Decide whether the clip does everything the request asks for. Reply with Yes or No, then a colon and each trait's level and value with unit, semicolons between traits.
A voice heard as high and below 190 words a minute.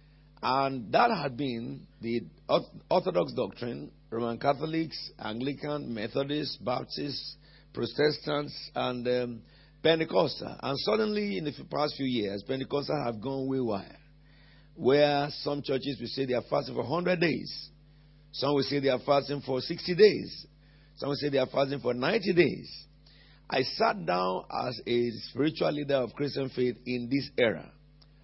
No: medium, 140 Hz; average, 150 wpm